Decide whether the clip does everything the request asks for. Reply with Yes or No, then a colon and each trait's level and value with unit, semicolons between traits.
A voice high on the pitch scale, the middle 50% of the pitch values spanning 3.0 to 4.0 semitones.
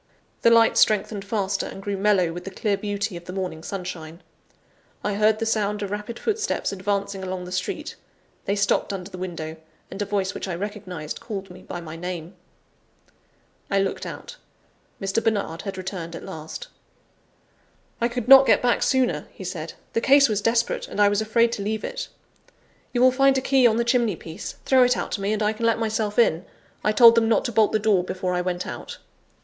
Yes: high, 205 Hz; average, 3.6 semitones